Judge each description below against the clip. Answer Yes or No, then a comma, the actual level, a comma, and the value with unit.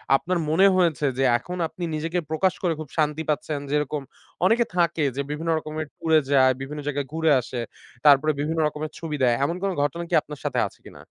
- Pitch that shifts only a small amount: Yes, narrow, 2.3 semitones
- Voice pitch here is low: No, medium, 155 Hz